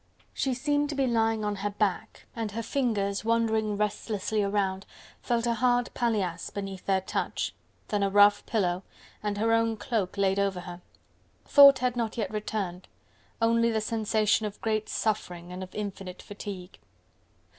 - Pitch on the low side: No, high, 210 Hz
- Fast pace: No, average, 160 wpm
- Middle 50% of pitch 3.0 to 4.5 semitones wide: No, narrow, 2.5 semitones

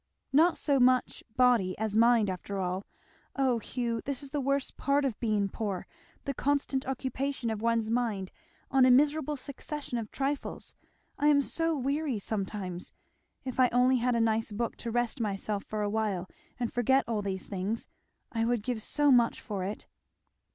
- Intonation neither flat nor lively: Yes, average, 4.1 semitones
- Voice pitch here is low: No, high, 240 Hz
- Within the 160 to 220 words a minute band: Yes, average, 175 wpm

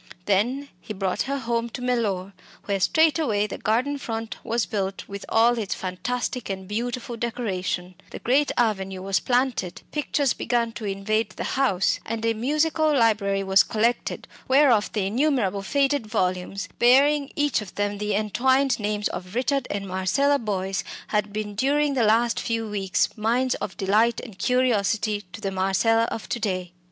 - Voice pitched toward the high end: Yes, high, 225 Hz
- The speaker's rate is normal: Yes, average, 165 wpm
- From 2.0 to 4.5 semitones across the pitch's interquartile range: Yes, average, 4.1 semitones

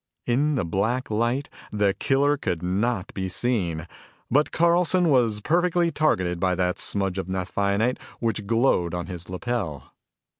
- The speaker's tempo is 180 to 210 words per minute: No, average, 145 wpm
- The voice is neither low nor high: No, low, 105 Hz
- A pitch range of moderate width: No, wide, 6.5 semitones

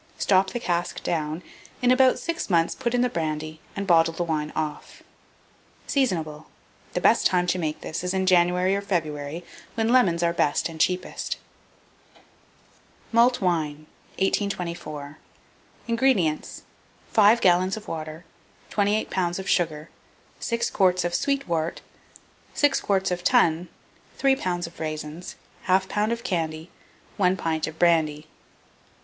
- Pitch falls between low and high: Yes, medium, 175 Hz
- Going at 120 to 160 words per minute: Yes, average, 140 wpm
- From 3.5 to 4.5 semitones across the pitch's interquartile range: Yes, average, 4.0 semitones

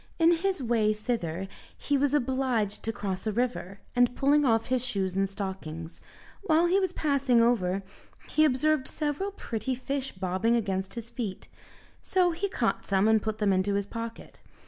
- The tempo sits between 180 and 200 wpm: No, average, 170 wpm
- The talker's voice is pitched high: Yes, high, 235 Hz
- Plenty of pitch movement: Yes, wide, 6.1 semitones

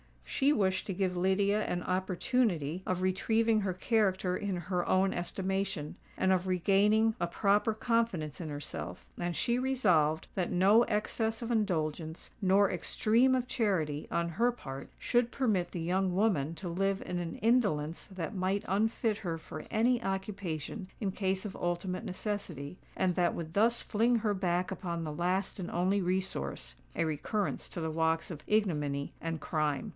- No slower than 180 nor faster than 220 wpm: No, average, 160 wpm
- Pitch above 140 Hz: Yes, medium, 185 Hz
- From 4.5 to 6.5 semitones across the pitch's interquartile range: No, average, 3.8 semitones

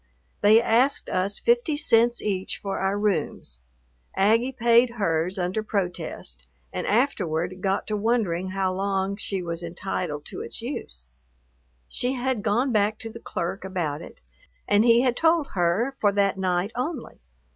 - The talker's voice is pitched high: Yes, high, 200 Hz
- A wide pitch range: No, average, 4.4 semitones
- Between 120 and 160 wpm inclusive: Yes, average, 155 wpm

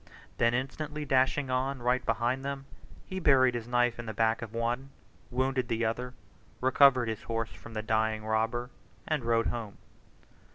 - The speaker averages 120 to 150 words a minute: No, average, 165 wpm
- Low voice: Yes, low, 120 Hz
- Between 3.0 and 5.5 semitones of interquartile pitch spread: No, narrow, 2.5 semitones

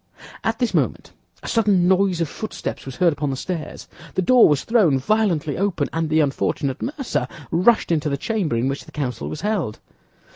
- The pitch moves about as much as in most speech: No, wide, 6.6 semitones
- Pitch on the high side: No, medium, 170 Hz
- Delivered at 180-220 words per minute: Yes, average, 190 wpm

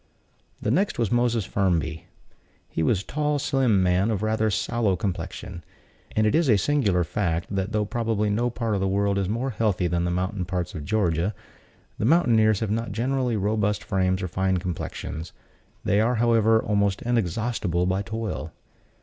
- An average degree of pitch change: Yes, average, 3.7 semitones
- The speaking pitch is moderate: No, low, 105 Hz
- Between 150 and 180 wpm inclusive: Yes, average, 175 wpm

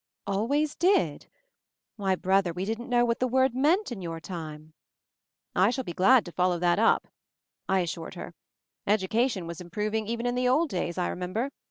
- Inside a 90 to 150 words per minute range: No, average, 185 wpm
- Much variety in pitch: Yes, wide, 5.7 semitones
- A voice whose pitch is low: No, high, 205 Hz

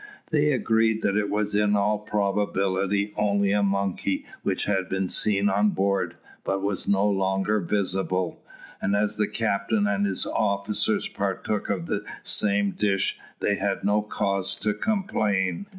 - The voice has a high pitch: No, low, 100 Hz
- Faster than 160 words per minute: No, average, 150 wpm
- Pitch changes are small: Yes, narrow, 1.4 semitones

